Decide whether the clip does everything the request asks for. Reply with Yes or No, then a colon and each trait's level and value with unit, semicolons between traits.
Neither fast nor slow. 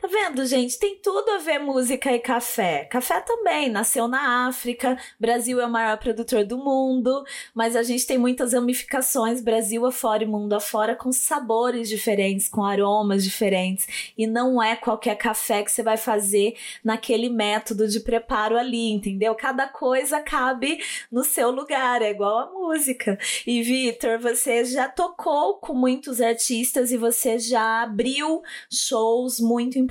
Yes: average, 160 wpm